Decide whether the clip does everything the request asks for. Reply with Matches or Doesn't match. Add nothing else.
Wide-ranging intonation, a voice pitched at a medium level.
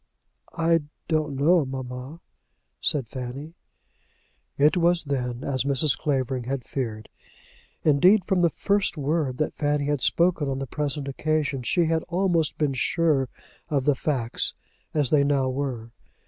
Doesn't match